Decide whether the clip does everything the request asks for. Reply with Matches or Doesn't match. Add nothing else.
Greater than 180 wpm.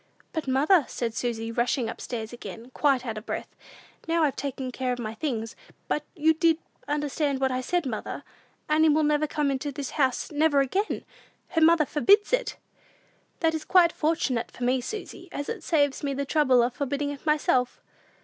Matches